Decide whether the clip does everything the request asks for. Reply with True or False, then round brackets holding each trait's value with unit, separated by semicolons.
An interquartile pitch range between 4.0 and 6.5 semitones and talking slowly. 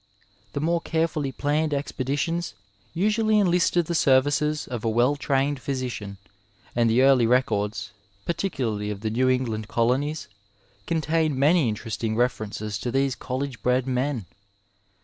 True (4.6 semitones; 130 wpm)